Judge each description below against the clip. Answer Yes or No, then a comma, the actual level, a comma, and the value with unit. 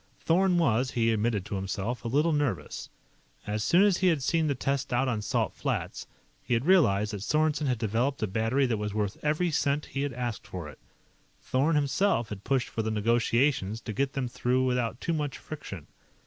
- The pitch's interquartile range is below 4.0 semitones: No, average, 5.2 semitones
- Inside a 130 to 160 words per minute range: No, fast, 205 wpm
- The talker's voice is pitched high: No, low, 125 Hz